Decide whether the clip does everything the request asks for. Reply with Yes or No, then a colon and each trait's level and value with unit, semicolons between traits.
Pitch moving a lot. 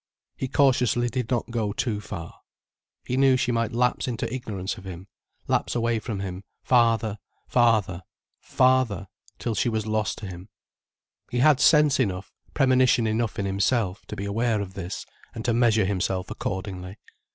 No: average, 3.8 semitones